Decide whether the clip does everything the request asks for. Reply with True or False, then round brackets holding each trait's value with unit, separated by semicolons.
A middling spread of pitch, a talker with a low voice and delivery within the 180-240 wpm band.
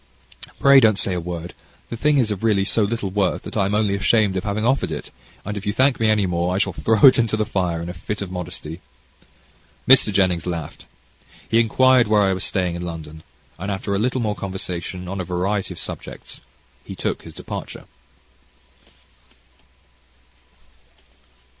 True (3.4 semitones; 100 Hz; 185 wpm)